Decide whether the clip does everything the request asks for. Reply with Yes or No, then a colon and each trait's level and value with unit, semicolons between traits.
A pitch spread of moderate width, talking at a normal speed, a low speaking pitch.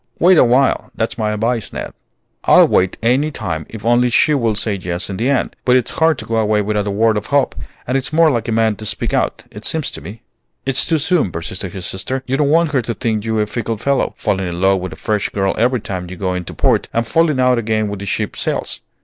No: average, 4.4 semitones; fast, 250 wpm; low, 115 Hz